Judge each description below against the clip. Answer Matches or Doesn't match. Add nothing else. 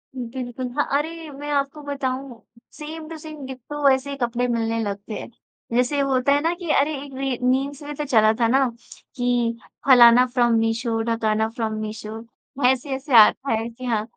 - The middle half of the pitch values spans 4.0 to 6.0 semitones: Doesn't match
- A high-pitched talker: Matches